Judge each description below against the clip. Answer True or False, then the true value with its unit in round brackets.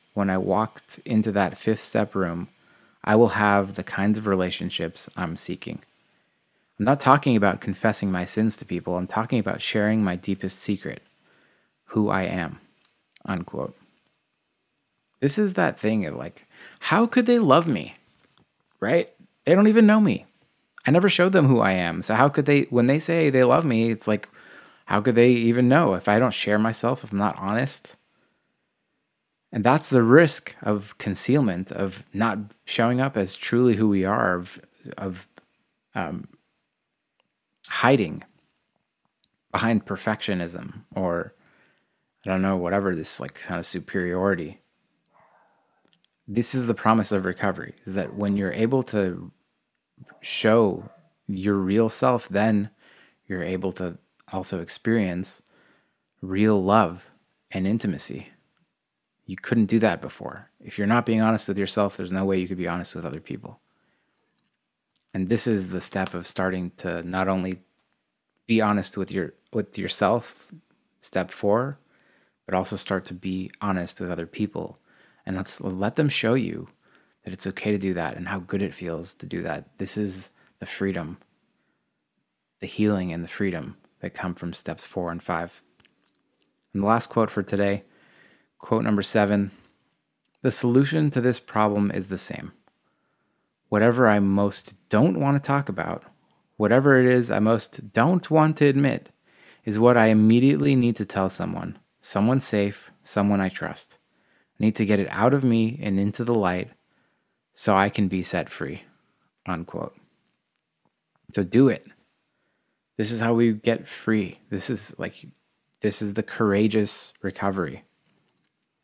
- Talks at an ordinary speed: True (160 wpm)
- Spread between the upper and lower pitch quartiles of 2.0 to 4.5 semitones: True (3.6 semitones)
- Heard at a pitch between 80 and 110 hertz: True (105 Hz)